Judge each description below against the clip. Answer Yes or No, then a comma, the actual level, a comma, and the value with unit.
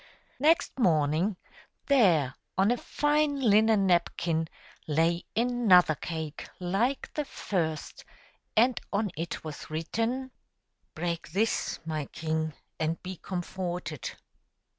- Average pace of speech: No, slow, 110 wpm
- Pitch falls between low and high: Yes, medium, 180 Hz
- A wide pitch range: Yes, wide, 6.1 semitones